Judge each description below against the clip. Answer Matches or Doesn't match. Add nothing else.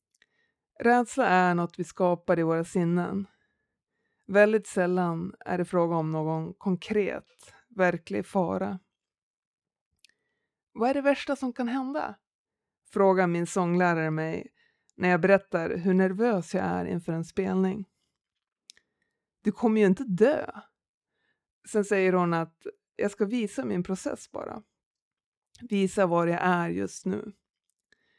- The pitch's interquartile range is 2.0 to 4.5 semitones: Matches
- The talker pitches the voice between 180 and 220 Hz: Matches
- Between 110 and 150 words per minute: Matches